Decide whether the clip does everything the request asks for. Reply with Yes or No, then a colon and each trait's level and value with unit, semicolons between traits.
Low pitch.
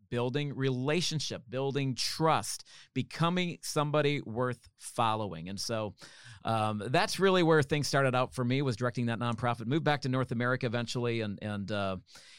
Yes: low, 125 Hz